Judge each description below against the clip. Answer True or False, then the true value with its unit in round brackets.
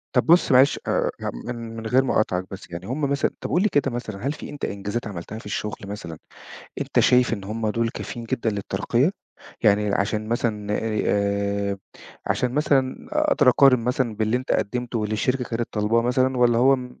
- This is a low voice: True (115 Hz)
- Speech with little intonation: False (3.5 semitones)